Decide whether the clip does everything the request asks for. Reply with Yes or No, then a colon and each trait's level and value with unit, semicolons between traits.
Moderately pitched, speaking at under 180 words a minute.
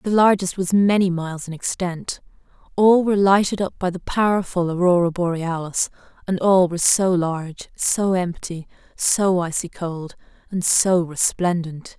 Yes: medium, 180 Hz; average, 145 wpm